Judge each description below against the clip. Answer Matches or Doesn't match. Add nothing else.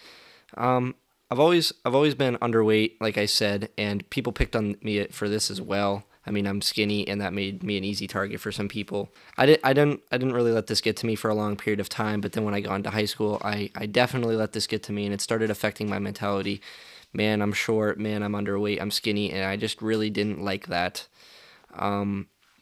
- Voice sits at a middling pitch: Doesn't match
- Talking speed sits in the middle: Doesn't match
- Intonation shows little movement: Matches